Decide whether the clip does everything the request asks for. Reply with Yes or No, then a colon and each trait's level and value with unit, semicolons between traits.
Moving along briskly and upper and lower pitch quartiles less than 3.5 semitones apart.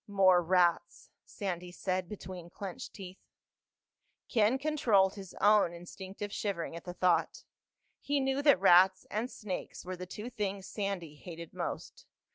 No: average, 140 wpm; average, 2.8 semitones